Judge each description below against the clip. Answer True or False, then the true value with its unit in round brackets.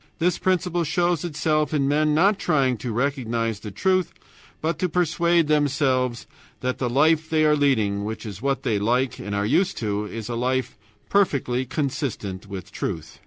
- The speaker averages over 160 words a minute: True (170 wpm)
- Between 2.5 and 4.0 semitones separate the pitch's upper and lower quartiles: False (5.6 semitones)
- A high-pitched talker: False (140 Hz)